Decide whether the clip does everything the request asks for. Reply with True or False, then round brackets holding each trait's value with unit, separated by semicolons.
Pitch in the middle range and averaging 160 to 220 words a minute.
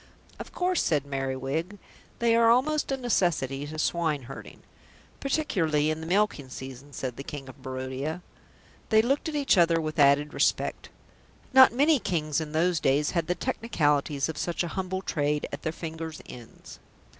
True (160 Hz; 165 wpm)